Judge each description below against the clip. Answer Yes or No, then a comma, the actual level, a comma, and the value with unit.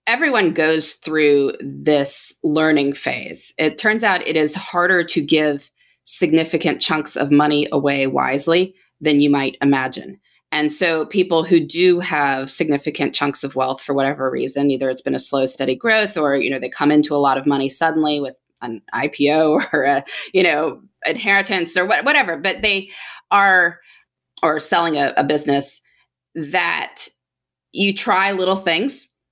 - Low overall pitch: No, medium, 150 Hz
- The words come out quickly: No, average, 160 wpm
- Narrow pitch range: No, average, 3.8 semitones